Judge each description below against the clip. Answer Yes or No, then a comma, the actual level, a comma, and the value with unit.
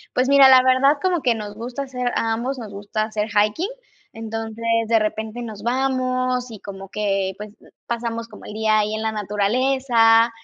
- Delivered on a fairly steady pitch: No, average, 3.1 semitones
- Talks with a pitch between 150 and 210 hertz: No, high, 225 Hz